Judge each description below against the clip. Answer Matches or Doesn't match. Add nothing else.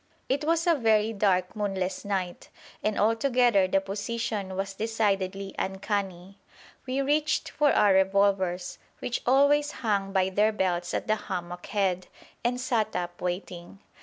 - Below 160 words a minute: Matches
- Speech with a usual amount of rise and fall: Matches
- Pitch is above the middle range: Matches